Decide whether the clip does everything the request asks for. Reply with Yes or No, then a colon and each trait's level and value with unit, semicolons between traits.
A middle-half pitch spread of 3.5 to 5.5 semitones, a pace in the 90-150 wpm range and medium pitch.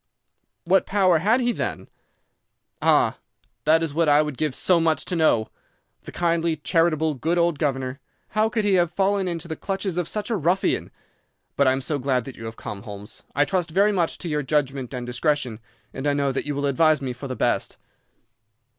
No: average, 4.4 semitones; average, 200 wpm; medium, 155 Hz